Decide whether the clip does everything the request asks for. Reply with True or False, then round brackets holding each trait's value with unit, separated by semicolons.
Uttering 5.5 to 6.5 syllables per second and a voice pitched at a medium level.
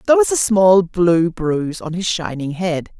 False (4.6 syllables/s; 180 Hz)